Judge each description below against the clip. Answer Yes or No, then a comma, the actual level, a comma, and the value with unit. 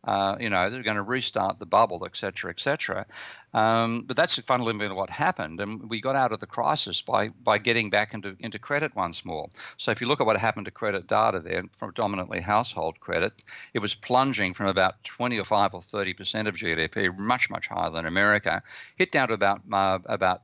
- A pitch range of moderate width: Yes, average, 3.2 semitones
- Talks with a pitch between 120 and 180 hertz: No, low, 105 Hz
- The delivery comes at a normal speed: No, fast, 210 wpm